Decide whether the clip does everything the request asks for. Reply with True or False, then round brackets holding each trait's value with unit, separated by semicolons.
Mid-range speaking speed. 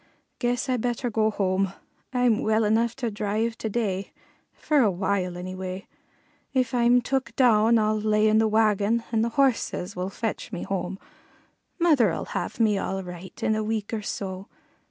True (170 wpm)